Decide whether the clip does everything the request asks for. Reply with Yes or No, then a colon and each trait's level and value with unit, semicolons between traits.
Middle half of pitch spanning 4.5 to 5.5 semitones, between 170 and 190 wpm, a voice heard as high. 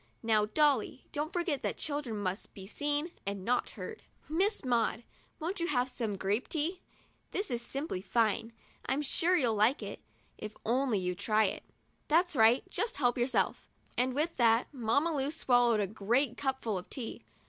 Yes: average, 5.2 semitones; average, 180 wpm; very high, 250 Hz